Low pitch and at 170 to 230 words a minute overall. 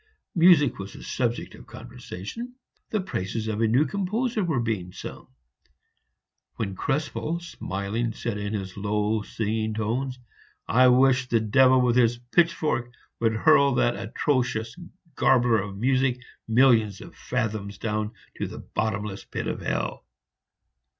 No: low, 115 Hz; slow, 135 wpm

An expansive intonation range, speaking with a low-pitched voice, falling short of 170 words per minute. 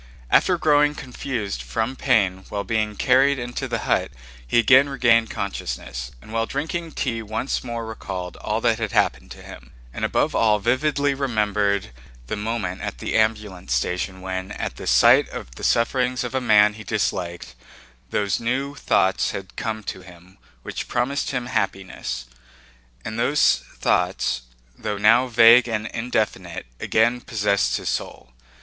No: average, 4.2 semitones; low, 110 Hz; average, 155 wpm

